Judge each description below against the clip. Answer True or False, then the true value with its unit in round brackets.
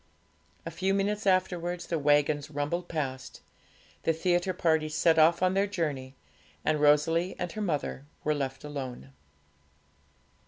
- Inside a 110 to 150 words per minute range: True (140 wpm)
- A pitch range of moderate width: True (3.4 semitones)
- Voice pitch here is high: False (160 Hz)